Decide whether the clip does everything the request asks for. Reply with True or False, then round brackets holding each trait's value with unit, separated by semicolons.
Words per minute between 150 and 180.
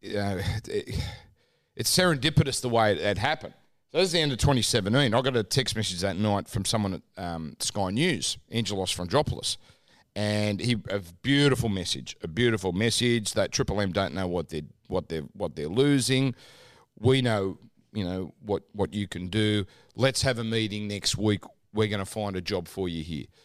False (190 wpm)